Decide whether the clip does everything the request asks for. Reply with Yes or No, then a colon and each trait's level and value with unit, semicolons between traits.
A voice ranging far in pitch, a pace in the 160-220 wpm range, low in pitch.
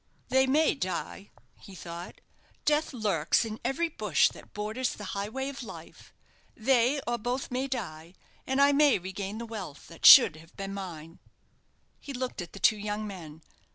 No: wide, 5.9 semitones; average, 170 wpm; high, 215 Hz